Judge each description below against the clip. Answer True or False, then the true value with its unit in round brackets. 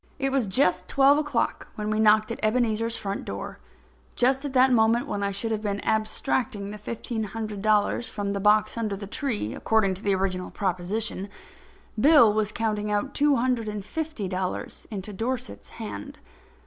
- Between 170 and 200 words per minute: True (175 wpm)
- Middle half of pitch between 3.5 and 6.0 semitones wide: False (3.0 semitones)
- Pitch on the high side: True (215 Hz)